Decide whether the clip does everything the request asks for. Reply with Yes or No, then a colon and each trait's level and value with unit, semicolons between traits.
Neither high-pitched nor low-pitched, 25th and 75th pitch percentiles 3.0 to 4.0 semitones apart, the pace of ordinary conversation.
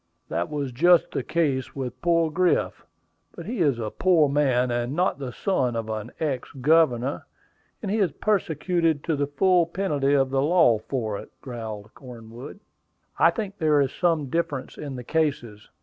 No: medium, 145 Hz; average, 5.2 semitones; average, 175 wpm